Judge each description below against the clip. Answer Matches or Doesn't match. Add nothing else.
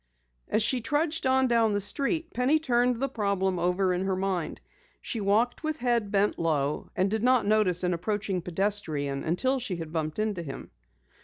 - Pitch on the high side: Matches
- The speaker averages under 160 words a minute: Doesn't match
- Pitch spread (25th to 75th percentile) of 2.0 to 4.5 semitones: Doesn't match